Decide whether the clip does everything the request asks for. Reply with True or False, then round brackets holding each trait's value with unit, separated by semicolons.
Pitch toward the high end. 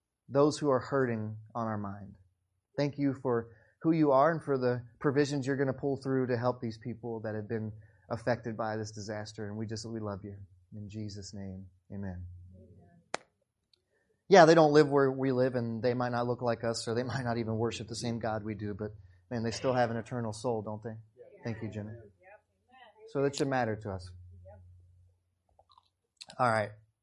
False (115 Hz)